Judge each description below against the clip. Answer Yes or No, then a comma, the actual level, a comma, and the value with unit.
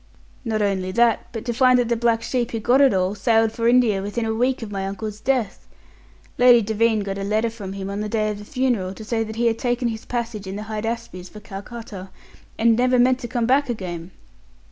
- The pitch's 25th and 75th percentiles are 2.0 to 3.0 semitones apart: Yes, average, 2.7 semitones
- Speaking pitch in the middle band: No, high, 225 Hz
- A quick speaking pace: Yes, fast, 230 wpm